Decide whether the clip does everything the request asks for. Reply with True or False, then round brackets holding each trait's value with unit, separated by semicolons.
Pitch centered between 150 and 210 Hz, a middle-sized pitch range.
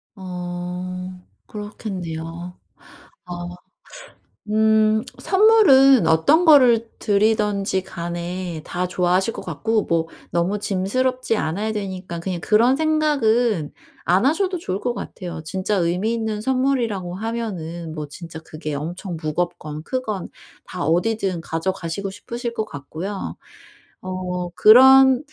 True (190 Hz; 4.6 semitones)